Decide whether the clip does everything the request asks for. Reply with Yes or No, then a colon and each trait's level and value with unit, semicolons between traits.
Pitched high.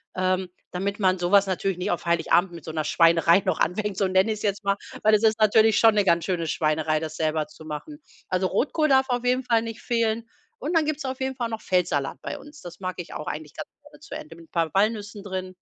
Yes: high, 195 Hz